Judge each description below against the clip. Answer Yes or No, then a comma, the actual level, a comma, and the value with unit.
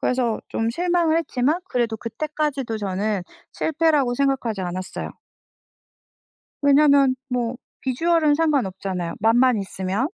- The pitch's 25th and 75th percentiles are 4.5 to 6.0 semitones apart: Yes, wide, 5.5 semitones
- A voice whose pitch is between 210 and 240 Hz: No, very high, 255 Hz